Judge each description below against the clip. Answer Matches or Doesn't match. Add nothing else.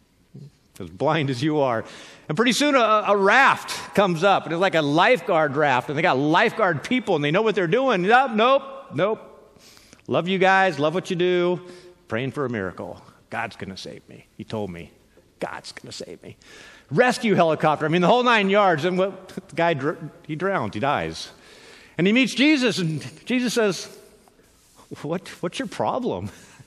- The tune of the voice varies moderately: Doesn't match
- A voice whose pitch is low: Doesn't match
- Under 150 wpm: Doesn't match